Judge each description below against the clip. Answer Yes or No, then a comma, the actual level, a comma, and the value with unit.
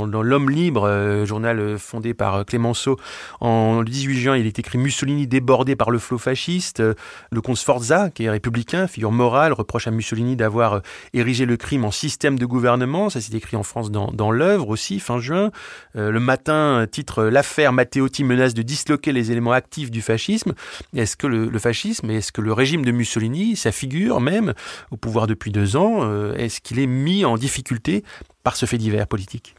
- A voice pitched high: No, low, 120 Hz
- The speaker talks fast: No, average, 185 wpm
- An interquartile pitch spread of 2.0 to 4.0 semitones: Yes, average, 3.6 semitones